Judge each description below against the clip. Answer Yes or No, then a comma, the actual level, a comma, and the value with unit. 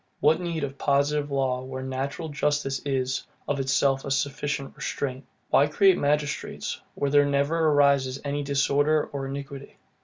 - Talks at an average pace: Yes, average, 150 wpm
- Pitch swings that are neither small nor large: No, narrow, 1.4 semitones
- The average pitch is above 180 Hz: No, medium, 140 Hz